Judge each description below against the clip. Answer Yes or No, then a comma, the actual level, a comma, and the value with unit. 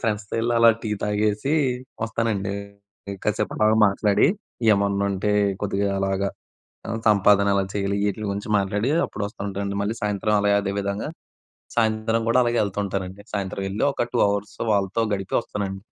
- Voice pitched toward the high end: No, low, 100 Hz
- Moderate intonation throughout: No, narrow, 1.6 semitones